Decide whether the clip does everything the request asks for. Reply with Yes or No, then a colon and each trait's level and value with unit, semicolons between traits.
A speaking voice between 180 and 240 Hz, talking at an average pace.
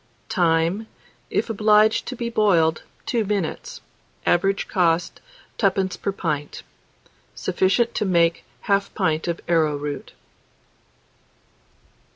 No: medium, 185 Hz; slow, 100 wpm